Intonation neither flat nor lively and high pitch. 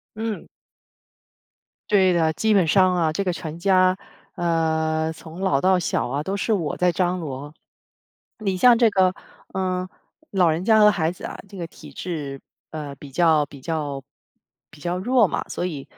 No: average, 3.1 semitones; medium, 175 Hz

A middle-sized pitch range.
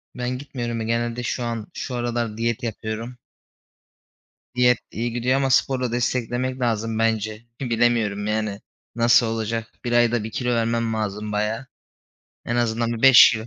No: narrow, 1.6 semitones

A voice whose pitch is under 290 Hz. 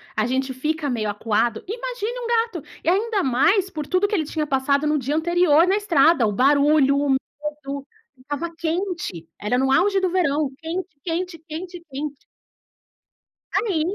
No: very high, 310 Hz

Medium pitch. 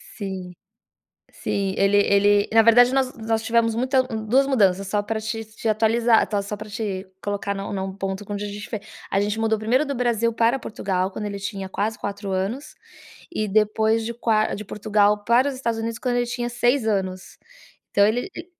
No: high, 215 Hz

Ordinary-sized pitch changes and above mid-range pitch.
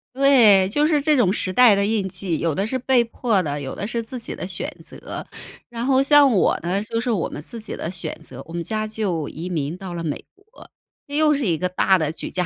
No: wide, 5.9 semitones; high, 205 Hz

